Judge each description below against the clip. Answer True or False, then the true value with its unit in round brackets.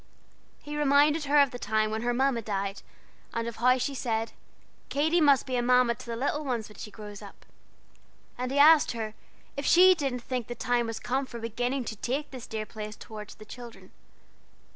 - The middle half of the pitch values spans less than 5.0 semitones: True (3.9 semitones)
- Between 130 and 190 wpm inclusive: False (205 wpm)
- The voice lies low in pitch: False (245 Hz)